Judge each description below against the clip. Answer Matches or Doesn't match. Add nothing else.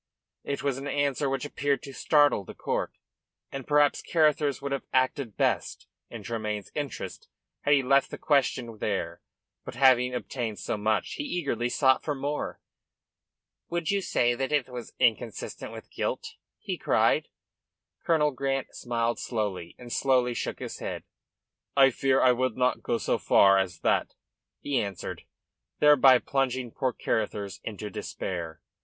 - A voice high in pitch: Doesn't match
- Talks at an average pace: Matches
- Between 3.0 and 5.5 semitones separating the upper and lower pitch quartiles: Matches